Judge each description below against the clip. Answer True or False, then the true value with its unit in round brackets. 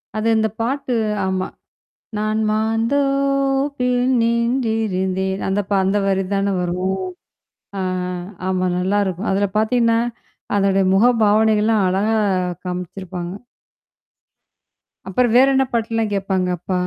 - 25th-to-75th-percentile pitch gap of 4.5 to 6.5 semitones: False (3.4 semitones)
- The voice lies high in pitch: True (215 Hz)